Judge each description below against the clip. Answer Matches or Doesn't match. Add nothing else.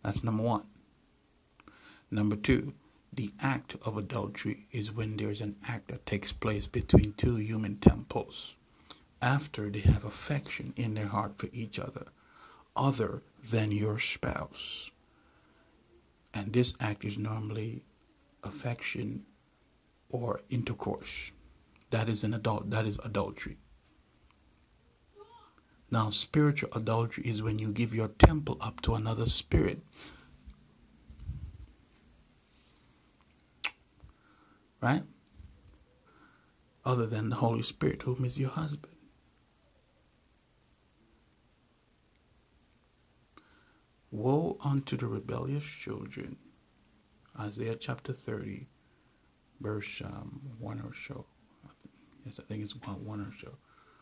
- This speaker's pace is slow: Matches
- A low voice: Matches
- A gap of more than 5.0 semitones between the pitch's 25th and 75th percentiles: Doesn't match